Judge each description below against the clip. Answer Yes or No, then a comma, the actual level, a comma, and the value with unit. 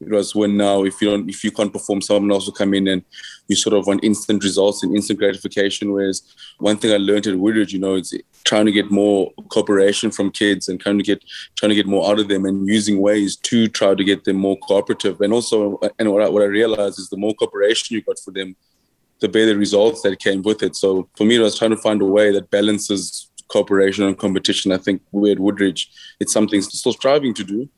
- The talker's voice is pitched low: Yes, low, 100 Hz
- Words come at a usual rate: No, fast, 245 wpm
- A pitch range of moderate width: No, narrow, 1.2 semitones